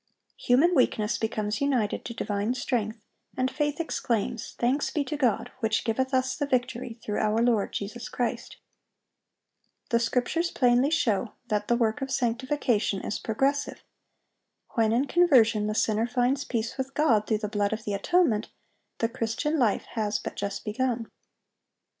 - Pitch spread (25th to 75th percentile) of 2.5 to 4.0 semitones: Yes, average, 3.4 semitones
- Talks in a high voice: Yes, high, 235 Hz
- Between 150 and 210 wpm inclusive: Yes, average, 155 wpm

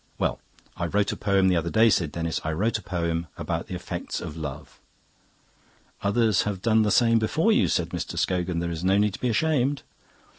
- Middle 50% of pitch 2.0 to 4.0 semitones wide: No, average, 4.7 semitones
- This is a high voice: No, very low, 95 Hz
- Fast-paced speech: Yes, fast, 210 wpm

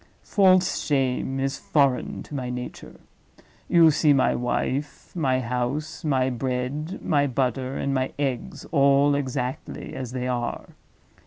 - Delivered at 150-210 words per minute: No, slow, 135 wpm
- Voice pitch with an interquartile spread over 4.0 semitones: No, narrow, 2.4 semitones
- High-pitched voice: No, low, 135 Hz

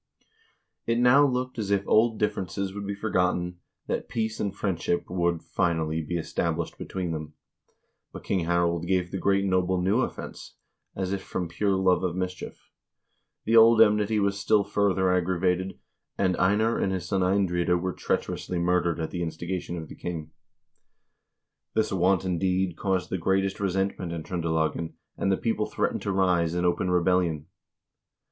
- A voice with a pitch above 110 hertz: No, very low, 95 Hz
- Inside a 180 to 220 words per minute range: No, average, 165 wpm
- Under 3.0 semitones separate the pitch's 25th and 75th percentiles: Yes, narrow, 2.4 semitones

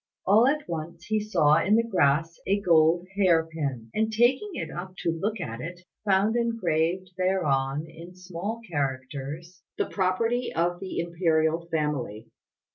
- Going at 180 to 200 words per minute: No, average, 150 wpm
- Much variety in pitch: No, average, 4.0 semitones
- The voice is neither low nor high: Yes, medium, 175 Hz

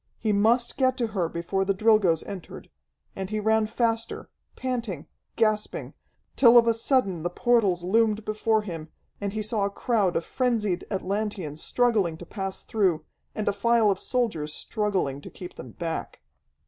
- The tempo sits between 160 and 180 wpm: Yes, average, 165 wpm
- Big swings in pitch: No, average, 3.7 semitones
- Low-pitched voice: No, high, 210 Hz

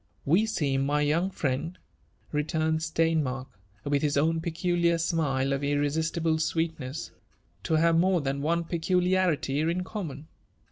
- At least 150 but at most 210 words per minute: No, average, 140 wpm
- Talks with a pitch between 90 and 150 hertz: No, medium, 160 Hz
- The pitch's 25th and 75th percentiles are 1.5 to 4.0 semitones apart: Yes, average, 2.8 semitones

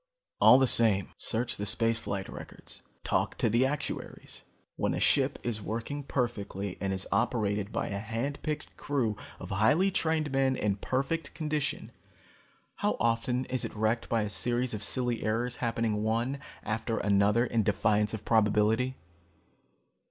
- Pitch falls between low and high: No, low, 115 Hz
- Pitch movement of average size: Yes, average, 3.5 semitones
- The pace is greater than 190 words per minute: No, average, 155 wpm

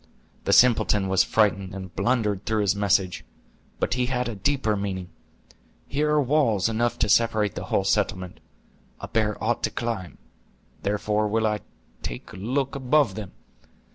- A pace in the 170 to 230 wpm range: No, average, 160 wpm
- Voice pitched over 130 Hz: No, low, 110 Hz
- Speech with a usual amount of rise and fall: Yes, average, 3.5 semitones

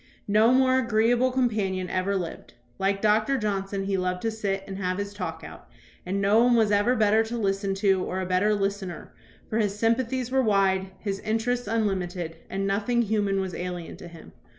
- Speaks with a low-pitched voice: No, high, 200 Hz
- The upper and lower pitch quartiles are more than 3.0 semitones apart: No, average, 2.7 semitones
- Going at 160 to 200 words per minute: Yes, average, 190 wpm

